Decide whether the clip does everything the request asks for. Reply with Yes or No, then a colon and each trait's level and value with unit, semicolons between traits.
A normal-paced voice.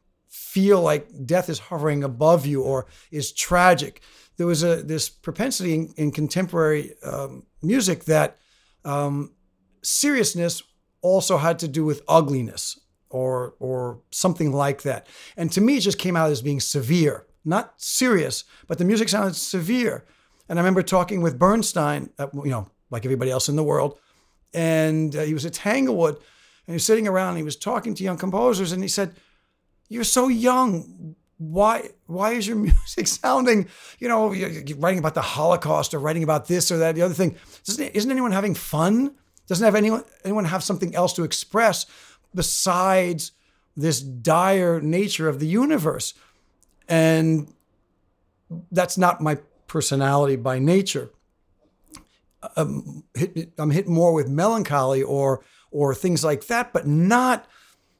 Yes: average, 160 wpm